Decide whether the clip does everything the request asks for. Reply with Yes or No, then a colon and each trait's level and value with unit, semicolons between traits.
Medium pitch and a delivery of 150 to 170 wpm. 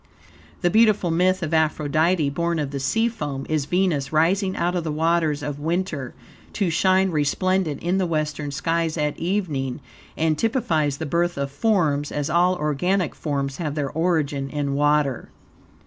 Yes: medium, 160 Hz; average, 165 wpm